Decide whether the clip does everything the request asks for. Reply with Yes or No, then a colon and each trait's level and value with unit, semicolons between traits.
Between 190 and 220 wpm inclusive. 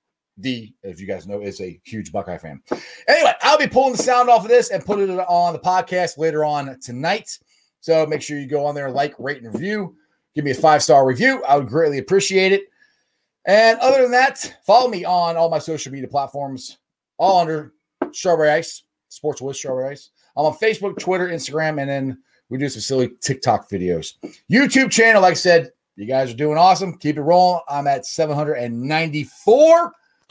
Yes: average, 195 wpm